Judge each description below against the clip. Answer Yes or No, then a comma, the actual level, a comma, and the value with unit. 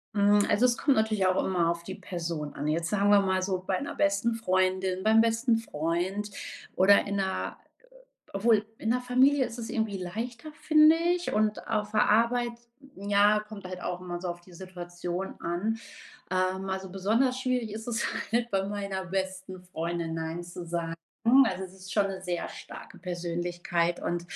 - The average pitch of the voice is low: No, high, 190 Hz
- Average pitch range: Yes, average, 3.8 semitones